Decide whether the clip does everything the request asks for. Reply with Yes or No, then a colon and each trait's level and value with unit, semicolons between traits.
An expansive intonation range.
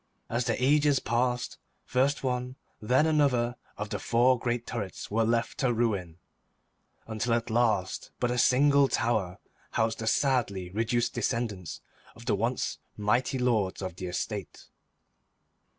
No: average, 2.9 semitones